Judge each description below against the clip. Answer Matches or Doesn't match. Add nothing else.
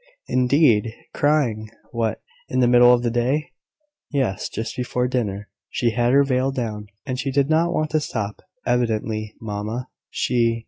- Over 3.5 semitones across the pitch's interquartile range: Doesn't match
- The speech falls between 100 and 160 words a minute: Matches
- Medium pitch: Doesn't match